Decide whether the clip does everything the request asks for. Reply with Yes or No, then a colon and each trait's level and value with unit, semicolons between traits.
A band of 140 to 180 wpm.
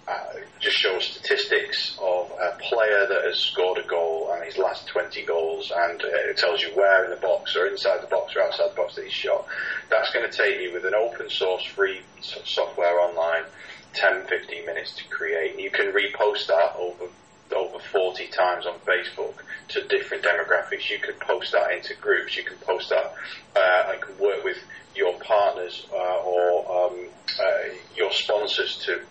No: average, 190 wpm